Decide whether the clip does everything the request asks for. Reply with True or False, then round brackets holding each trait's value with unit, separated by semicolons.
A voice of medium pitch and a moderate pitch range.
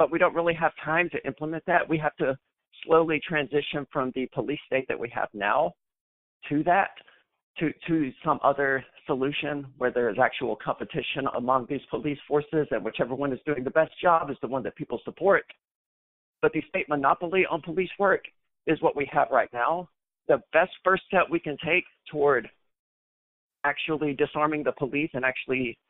True (150 Hz; 3.4 semitones)